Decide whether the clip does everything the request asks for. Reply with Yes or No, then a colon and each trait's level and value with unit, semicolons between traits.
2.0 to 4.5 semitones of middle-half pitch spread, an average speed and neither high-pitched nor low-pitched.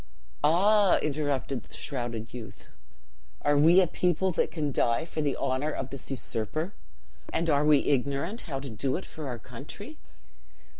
Yes: average, 4.0 semitones; average, 160 wpm; medium, 145 Hz